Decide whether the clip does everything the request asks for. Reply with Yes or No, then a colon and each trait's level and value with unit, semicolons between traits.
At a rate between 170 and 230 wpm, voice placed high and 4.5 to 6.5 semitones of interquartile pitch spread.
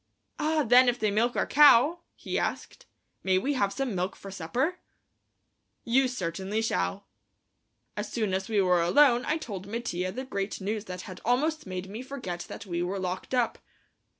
Yes: average, 180 wpm; high, 215 Hz; wide, 5.4 semitones